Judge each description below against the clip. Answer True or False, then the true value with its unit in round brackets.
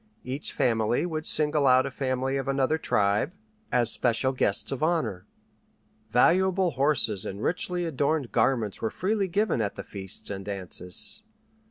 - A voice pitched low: True (130 Hz)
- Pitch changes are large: True (6.3 semitones)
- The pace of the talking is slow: False (150 wpm)